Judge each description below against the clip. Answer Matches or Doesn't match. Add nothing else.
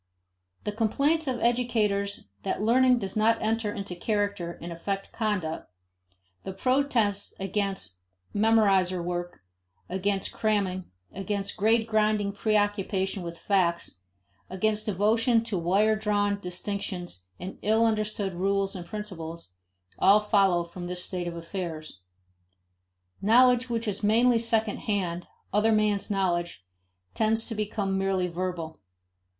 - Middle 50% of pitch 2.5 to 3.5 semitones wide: Matches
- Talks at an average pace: Doesn't match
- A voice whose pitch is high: Matches